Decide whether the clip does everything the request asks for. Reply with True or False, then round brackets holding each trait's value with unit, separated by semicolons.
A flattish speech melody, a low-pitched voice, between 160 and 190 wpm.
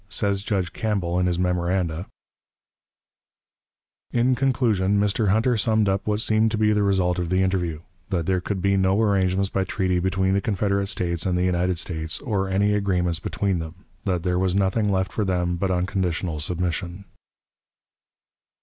True (2.2 semitones; 95 Hz; 170 wpm)